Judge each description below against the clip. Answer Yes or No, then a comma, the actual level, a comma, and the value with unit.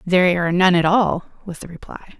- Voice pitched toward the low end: No, medium, 180 Hz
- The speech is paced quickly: Yes, fast, 220 wpm